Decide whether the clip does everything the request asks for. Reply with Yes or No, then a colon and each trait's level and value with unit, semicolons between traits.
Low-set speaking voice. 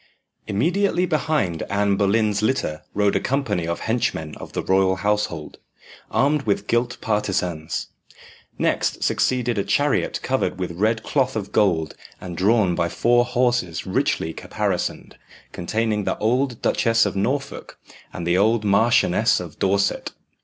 Yes: low, 105 Hz